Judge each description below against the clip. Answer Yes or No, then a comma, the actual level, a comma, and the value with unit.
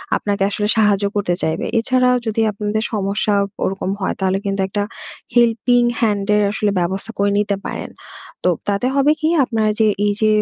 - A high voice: Yes, high, 210 Hz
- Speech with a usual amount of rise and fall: No, narrow, 2.1 semitones